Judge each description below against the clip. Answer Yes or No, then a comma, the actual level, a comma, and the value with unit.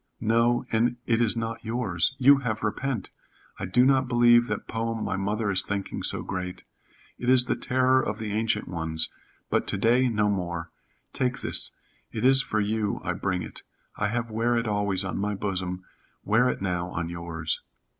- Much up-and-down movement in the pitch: No, average, 4.1 semitones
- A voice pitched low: Yes, low, 110 Hz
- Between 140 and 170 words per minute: No, average, 185 wpm